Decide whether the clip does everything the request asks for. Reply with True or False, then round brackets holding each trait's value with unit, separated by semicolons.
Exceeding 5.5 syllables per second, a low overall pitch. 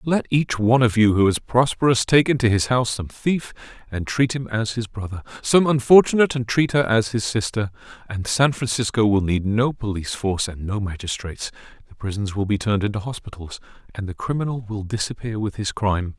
True (5.8 syllables/s; 110 Hz)